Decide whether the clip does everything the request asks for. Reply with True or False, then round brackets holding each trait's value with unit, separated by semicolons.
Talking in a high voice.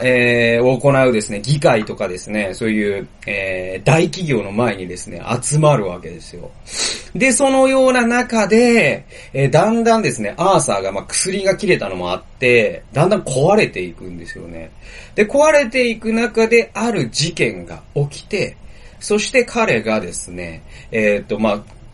False (135 Hz)